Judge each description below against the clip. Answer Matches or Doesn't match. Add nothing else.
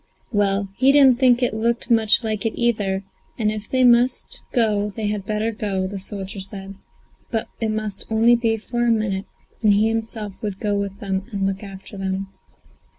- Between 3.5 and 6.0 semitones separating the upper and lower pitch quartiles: Doesn't match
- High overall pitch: Matches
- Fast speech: Doesn't match